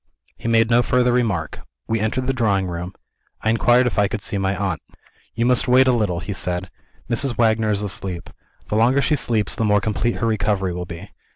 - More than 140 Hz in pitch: No, low, 110 Hz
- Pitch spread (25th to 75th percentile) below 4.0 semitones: Yes, average, 3.6 semitones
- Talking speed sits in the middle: No, fast, 210 wpm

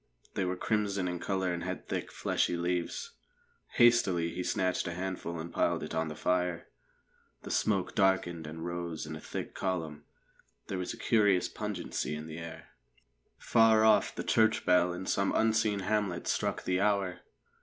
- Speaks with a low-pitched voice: Yes, very low, 90 Hz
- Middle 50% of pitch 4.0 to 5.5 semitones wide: No, average, 2.9 semitones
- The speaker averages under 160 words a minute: No, average, 170 wpm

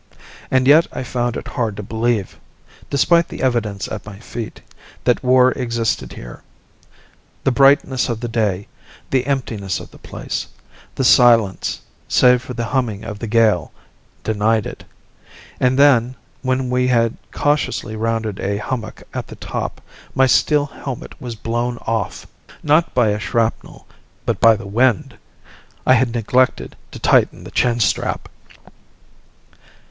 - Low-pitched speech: Yes, low, 120 Hz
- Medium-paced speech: Yes, average, 145 wpm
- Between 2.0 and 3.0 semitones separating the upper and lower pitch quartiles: Yes, average, 2.7 semitones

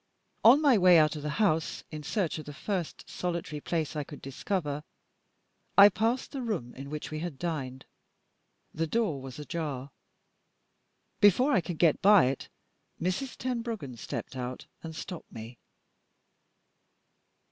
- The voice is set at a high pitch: No, medium, 160 Hz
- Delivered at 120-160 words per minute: Yes, average, 150 wpm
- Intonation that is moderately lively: No, wide, 5.8 semitones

